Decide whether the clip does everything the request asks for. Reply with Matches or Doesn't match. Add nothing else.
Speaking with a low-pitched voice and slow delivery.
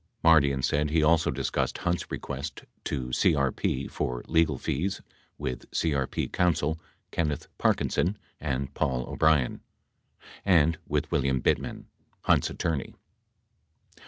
Matches